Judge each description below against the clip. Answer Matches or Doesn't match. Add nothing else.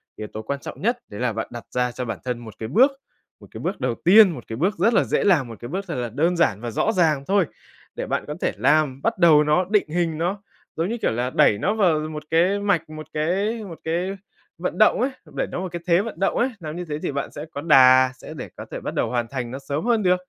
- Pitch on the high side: Doesn't match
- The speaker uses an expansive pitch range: Matches